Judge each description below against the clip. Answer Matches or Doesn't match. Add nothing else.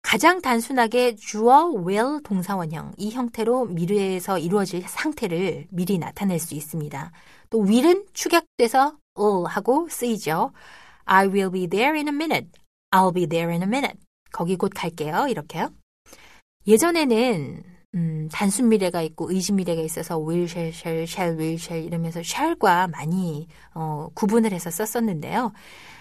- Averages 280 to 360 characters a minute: Doesn't match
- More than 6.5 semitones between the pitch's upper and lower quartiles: Doesn't match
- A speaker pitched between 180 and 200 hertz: Matches